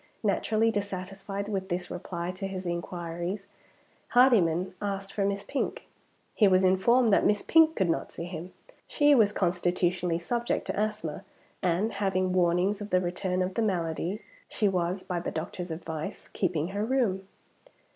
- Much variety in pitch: No, average, 2.8 semitones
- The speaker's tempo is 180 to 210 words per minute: No, average, 155 wpm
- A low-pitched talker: No, high, 190 Hz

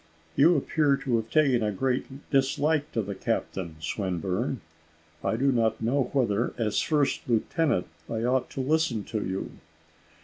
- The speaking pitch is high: No, low, 125 Hz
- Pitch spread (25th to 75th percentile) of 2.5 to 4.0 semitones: No, average, 4.5 semitones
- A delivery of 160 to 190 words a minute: No, average, 150 wpm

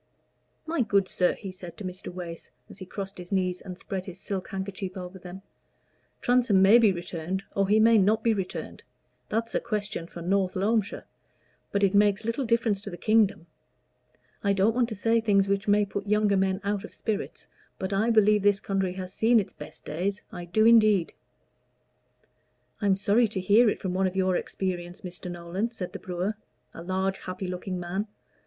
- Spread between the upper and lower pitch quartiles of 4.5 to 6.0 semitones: No, narrow, 2.4 semitones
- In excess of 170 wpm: Yes, average, 195 wpm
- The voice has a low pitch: No, high, 195 Hz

